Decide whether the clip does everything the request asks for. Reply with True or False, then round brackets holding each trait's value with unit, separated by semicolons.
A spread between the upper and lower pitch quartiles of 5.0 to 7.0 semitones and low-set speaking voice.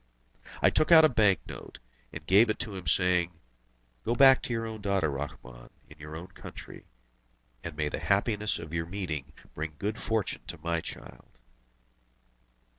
True (5.6 semitones; 90 Hz)